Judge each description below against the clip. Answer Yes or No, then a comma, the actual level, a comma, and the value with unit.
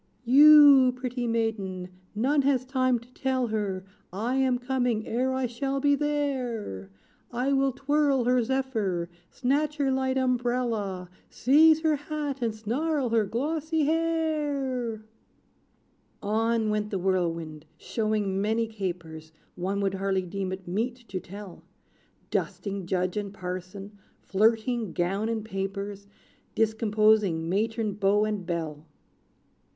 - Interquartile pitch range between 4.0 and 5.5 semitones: Yes, average, 5.2 semitones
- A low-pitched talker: No, high, 225 Hz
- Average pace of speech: No, slow, 125 wpm